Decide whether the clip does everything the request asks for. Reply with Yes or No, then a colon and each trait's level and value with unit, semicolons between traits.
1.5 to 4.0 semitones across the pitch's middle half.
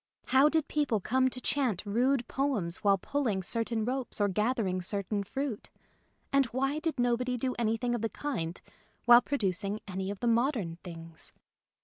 No: average, 4.7 semitones